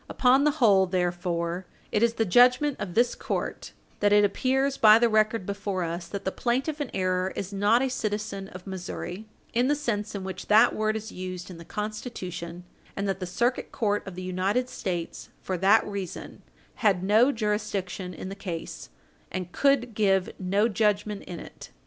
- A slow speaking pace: No, average, 185 wpm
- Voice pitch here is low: No, high, 205 Hz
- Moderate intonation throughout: Yes, average, 3.6 semitones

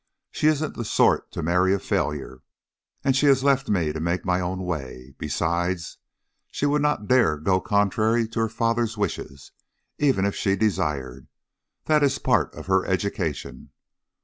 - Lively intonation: Yes, wide, 5.8 semitones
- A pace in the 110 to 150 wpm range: No, average, 165 wpm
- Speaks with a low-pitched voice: Yes, very low, 95 Hz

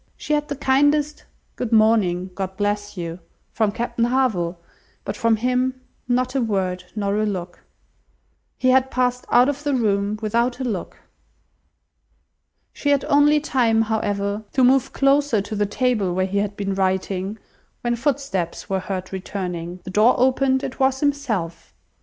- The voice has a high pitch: Yes, high, 225 Hz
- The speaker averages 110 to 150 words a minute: No, average, 160 wpm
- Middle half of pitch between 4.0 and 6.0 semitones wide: Yes, average, 5.0 semitones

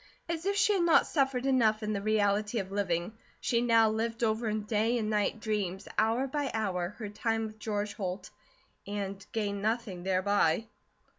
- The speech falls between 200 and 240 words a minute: No, average, 175 wpm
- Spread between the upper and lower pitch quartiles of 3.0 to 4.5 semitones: No, narrow, 2.4 semitones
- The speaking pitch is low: No, high, 215 Hz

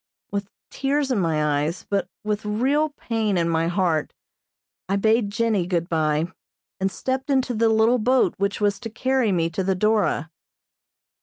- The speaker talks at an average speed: Yes, average, 165 wpm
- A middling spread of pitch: Yes, average, 5.0 semitones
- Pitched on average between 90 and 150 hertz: No, high, 205 Hz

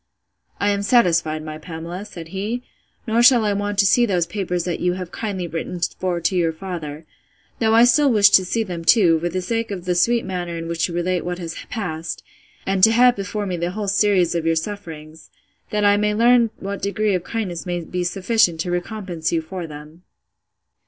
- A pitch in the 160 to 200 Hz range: Yes, medium, 185 Hz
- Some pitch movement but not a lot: Yes, average, 3.5 semitones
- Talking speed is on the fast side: Yes, fast, 210 wpm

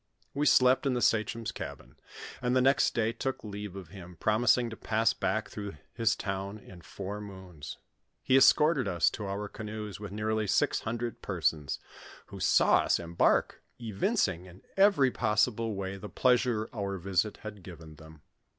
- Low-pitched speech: Yes, low, 105 Hz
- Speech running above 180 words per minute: No, average, 165 wpm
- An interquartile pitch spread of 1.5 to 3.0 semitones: No, average, 3.7 semitones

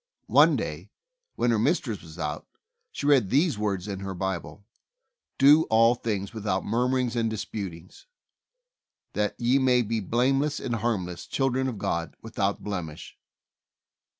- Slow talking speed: No, average, 150 wpm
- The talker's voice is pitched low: Yes, low, 110 Hz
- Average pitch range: Yes, average, 4.5 semitones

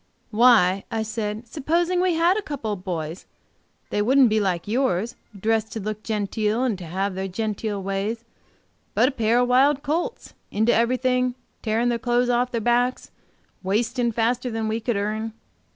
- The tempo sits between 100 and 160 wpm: No, average, 175 wpm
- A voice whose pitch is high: Yes, high, 225 Hz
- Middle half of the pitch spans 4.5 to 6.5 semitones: No, average, 3.1 semitones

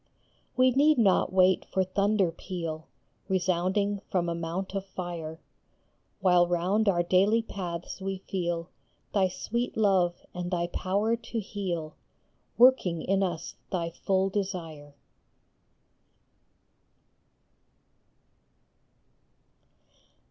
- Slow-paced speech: Yes, slow, 100 wpm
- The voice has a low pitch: No, medium, 185 Hz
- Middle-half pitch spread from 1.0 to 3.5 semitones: Yes, narrow, 2.6 semitones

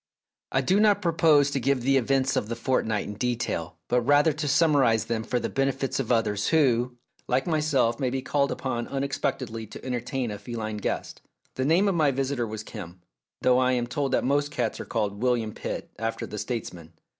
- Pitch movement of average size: Yes, average, 3.5 semitones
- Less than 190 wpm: No, average, 200 wpm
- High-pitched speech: No, low, 125 Hz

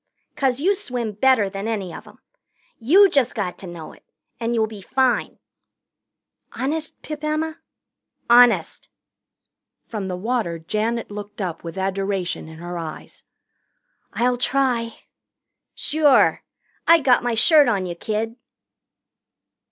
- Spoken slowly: Yes, slow, 130 wpm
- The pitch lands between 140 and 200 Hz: No, high, 230 Hz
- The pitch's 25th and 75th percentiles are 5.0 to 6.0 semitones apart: Yes, average, 5.3 semitones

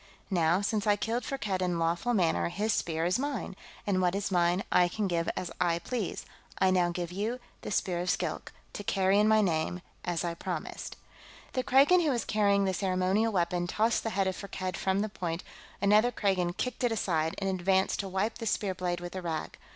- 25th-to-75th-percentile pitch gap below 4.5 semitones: Yes, average, 3.2 semitones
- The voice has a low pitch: No, high, 190 Hz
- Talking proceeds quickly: Yes, fast, 210 wpm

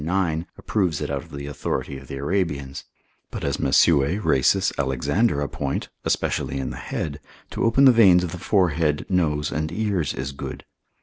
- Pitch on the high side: No, very low, 80 Hz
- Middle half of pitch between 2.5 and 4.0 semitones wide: No, average, 4.6 semitones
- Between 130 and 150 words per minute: No, average, 175 wpm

